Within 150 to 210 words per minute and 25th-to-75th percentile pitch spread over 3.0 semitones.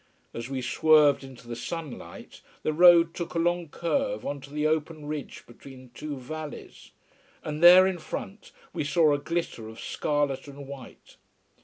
Yes: average, 165 wpm; average, 3.5 semitones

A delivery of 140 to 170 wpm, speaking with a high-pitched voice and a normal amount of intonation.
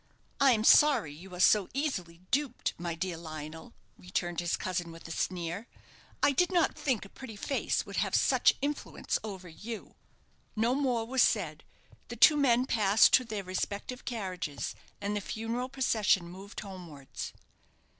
No: average, 160 wpm; high, 205 Hz; wide, 6.2 semitones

